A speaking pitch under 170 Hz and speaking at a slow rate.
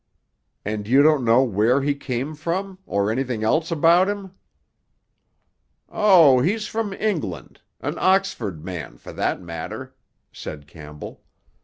Yes: low, 135 Hz; slow, 125 wpm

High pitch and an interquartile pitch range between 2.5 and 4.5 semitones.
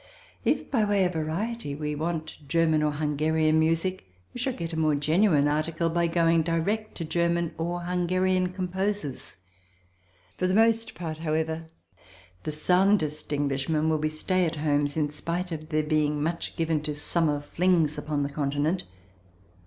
No: medium, 160 Hz; average, 2.8 semitones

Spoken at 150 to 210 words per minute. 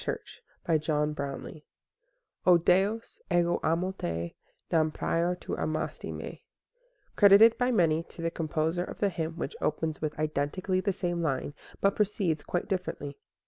No: average, 140 wpm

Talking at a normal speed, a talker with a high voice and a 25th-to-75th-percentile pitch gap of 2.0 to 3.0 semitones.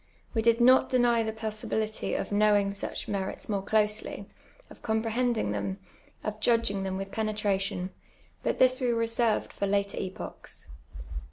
Yes: average, 145 wpm; high, 215 Hz; narrow, 2.5 semitones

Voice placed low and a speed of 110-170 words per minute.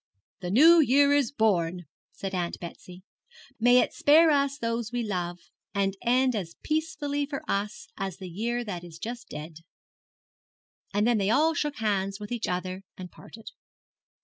No: high, 220 Hz; average, 165 wpm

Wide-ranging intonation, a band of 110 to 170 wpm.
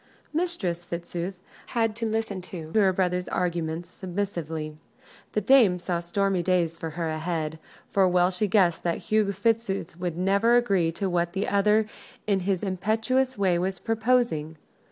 No: average, 3.6 semitones; average, 155 wpm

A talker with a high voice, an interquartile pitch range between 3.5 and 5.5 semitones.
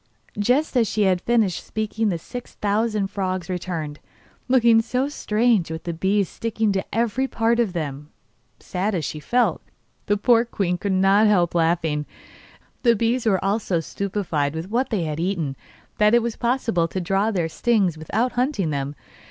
Yes: high, 200 Hz; average, 4.9 semitones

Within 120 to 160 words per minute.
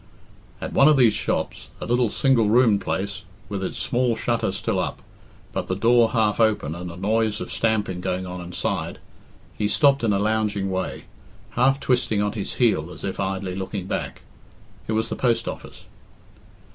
No: average, 180 wpm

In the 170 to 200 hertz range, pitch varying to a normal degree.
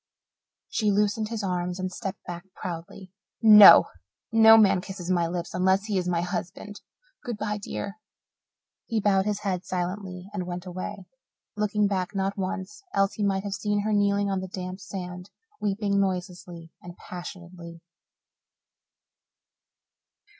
No: high, 190 Hz; narrow, 2.3 semitones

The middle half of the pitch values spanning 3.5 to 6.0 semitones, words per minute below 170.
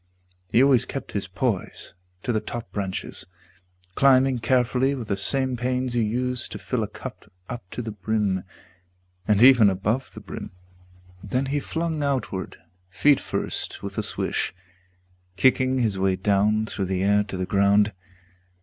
Yes: average, 4.5 semitones; average, 160 wpm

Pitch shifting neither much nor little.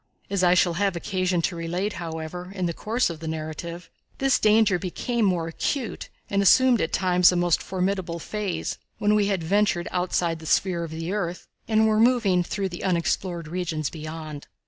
Yes: average, 3.2 semitones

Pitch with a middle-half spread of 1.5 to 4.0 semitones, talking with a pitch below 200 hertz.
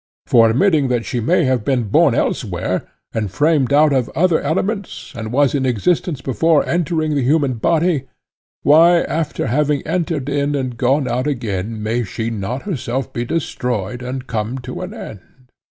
No: average, 4.7 semitones; low, 135 Hz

